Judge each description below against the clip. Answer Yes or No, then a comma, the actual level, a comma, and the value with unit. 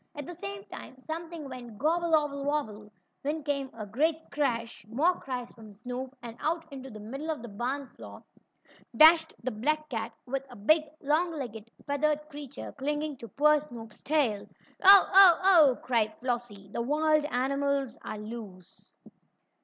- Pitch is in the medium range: No, very high, 275 Hz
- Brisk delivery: No, average, 160 wpm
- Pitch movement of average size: Yes, average, 4.8 semitones